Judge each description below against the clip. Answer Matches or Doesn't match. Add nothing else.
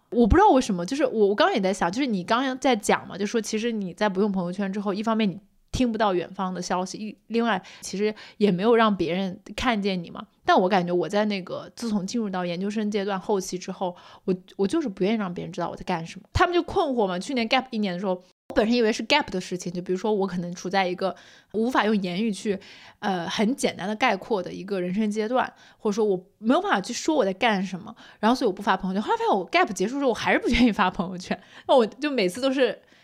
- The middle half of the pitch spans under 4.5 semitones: Matches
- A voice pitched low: Doesn't match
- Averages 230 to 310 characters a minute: Doesn't match